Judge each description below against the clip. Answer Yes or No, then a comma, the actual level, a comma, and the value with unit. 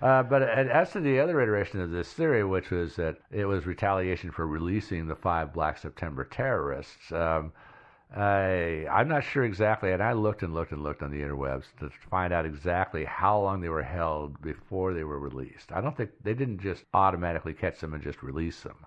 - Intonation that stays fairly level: No, average, 4.3 semitones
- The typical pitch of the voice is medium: No, very low, 90 Hz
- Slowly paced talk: No, fast, 205 wpm